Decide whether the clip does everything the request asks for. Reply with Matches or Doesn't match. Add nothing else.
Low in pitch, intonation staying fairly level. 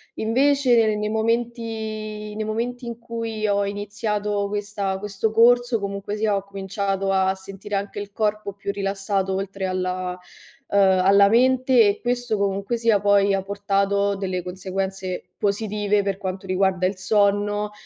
Doesn't match